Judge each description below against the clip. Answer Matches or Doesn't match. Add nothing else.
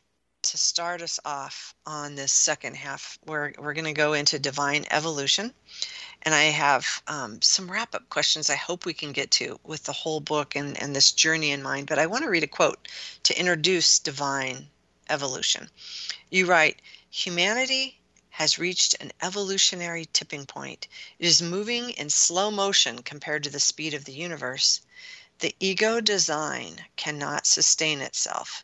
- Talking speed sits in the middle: Matches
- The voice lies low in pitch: Doesn't match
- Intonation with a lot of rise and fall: Doesn't match